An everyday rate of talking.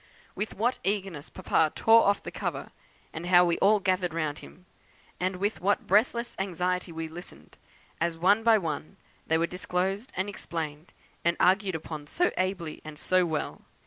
Yes: average, 170 wpm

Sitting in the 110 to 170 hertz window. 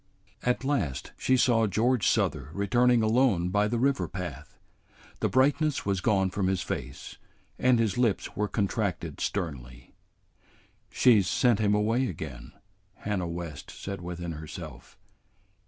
No: low, 100 Hz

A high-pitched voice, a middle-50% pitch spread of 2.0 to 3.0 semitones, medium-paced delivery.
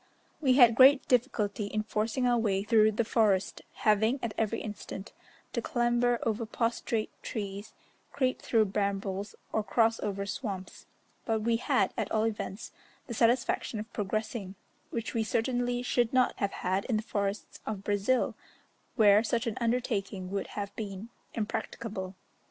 Yes: high, 220 Hz; average, 2.7 semitones; average, 150 wpm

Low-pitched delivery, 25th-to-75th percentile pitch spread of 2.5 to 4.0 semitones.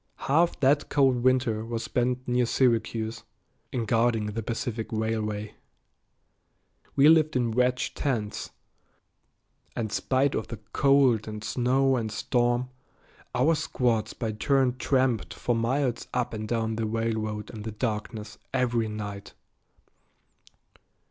Yes: low, 115 Hz; average, 2.8 semitones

